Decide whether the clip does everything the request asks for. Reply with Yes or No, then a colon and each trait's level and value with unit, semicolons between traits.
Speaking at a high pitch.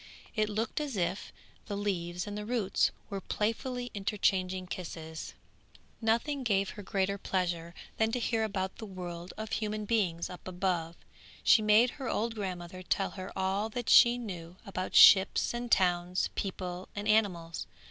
Yes: high, 195 Hz